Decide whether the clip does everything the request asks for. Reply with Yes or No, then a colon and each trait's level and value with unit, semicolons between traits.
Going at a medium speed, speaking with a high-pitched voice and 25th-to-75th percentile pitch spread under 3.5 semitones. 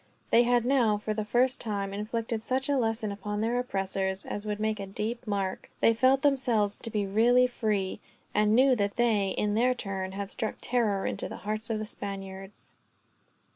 Yes: average, 190 wpm; high, 215 Hz; average, 3.1 semitones